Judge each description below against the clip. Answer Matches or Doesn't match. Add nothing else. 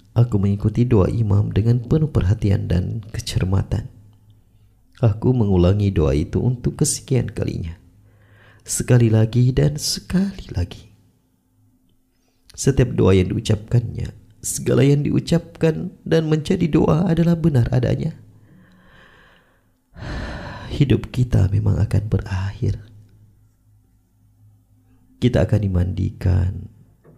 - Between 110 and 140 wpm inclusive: Doesn't match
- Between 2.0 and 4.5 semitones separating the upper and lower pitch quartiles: Matches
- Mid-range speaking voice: Doesn't match